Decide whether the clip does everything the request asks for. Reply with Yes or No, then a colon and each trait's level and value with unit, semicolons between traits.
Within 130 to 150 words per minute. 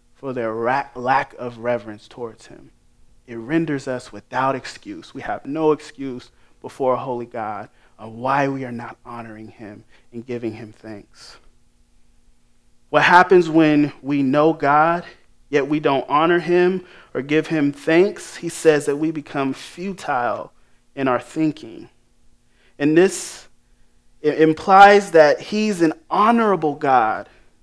Yes: slow, 135 wpm